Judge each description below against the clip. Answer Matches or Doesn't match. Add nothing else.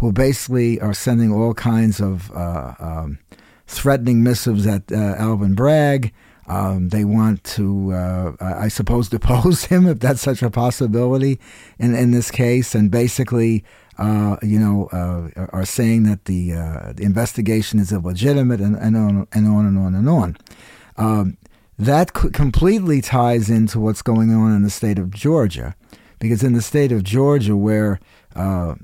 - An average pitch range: Matches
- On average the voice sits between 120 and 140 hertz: Doesn't match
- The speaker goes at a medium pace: Matches